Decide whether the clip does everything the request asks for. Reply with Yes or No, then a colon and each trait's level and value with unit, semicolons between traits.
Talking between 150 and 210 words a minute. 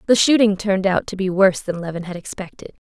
No: fast, 230 wpm